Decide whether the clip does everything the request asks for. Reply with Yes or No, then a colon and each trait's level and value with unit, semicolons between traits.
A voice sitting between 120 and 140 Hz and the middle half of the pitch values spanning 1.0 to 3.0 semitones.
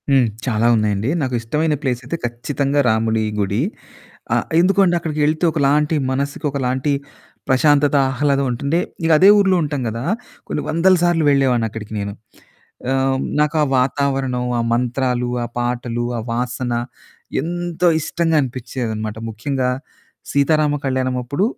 No: low, 135 Hz; average, 3.7 semitones